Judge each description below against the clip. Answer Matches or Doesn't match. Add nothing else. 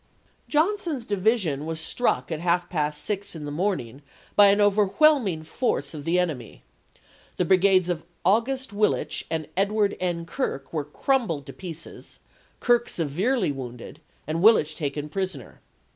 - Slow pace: Doesn't match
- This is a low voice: Doesn't match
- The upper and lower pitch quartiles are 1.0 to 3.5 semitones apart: Doesn't match